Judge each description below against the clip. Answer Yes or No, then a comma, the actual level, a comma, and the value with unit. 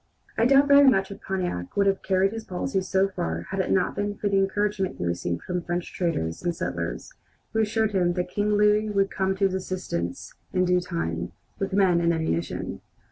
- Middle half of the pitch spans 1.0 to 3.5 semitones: Yes, average, 2.8 semitones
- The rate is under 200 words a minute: No, fast, 205 wpm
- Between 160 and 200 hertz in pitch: Yes, high, 190 Hz